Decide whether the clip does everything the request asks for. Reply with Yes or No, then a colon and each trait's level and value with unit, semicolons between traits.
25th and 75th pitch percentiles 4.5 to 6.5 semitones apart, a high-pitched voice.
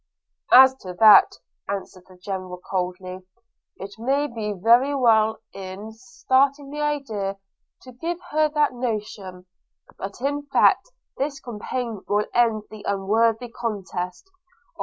Yes: average, 5.1 semitones; high, 225 Hz